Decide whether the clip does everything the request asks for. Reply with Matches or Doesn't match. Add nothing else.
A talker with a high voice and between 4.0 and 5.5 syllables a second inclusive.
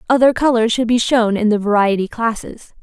Matches